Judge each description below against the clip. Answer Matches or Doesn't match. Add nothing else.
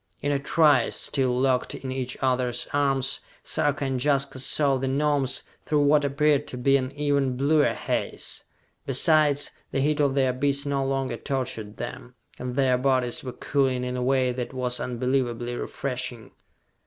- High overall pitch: Doesn't match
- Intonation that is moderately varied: Doesn't match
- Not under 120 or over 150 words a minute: Doesn't match